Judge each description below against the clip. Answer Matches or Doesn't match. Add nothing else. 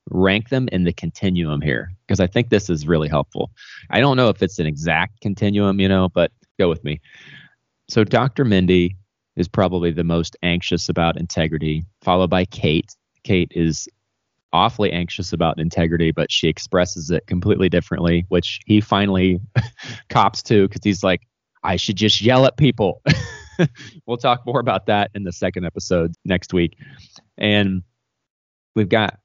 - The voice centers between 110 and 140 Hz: Doesn't match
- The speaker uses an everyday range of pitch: Matches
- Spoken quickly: Doesn't match